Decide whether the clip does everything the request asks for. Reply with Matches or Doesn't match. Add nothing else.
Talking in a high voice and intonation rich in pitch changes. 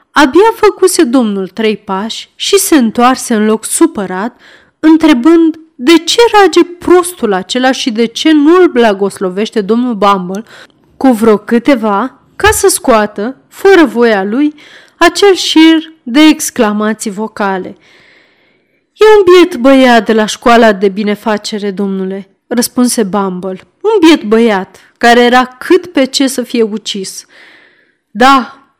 Matches